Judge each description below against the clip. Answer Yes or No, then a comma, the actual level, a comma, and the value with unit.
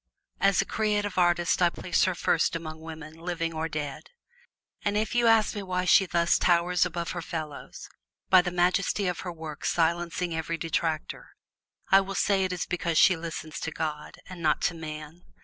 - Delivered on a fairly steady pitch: Yes, narrow, 2.3 semitones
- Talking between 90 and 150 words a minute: No, average, 185 wpm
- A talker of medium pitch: Yes, medium, 170 Hz